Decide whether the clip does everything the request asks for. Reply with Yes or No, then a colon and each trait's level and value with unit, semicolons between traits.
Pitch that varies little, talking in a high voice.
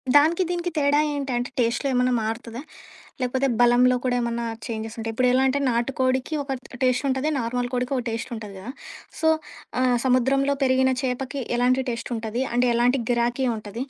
Yes: narrow, 1.9 semitones; very high, 250 Hz